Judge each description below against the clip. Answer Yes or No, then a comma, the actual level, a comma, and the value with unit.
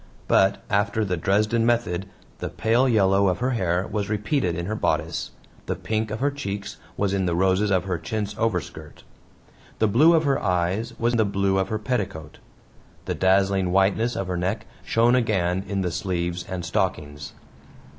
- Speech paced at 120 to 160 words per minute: No, average, 175 wpm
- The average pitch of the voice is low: Yes, low, 100 Hz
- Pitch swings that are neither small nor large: Yes, average, 3.4 semitones